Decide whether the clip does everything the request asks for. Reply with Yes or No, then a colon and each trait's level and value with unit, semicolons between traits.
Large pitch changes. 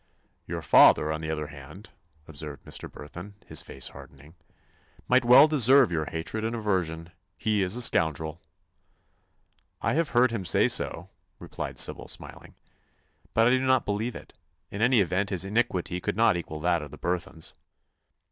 Yes: wide, 6.4 semitones